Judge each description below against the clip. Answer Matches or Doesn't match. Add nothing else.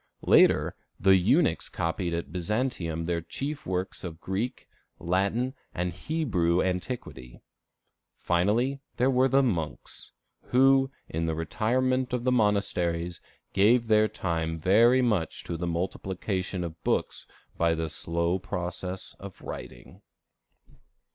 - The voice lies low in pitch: Matches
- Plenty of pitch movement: Matches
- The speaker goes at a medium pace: Doesn't match